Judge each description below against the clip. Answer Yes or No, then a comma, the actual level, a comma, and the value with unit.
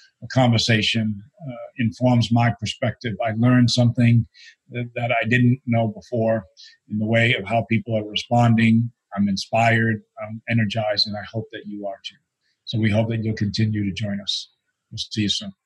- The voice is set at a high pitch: No, low, 115 Hz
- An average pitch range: No, narrow, 1.9 semitones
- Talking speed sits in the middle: Yes, average, 180 wpm